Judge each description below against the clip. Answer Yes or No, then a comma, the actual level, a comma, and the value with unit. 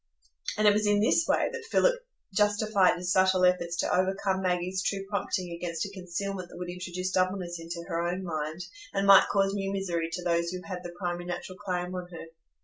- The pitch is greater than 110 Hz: Yes, medium, 185 Hz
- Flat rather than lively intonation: Yes, narrow, 1.9 semitones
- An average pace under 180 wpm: No, fast, 205 wpm